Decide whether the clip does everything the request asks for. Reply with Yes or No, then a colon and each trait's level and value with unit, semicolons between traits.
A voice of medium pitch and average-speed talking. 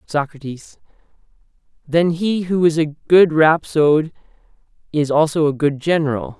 No: medium, 155 Hz; slow, 120 wpm